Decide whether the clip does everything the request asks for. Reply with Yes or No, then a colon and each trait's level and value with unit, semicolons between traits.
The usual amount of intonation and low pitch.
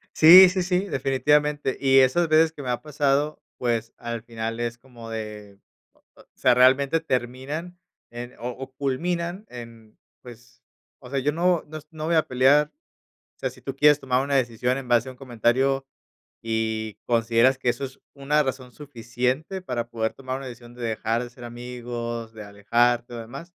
Yes: average, 3.6 semitones; low, 130 Hz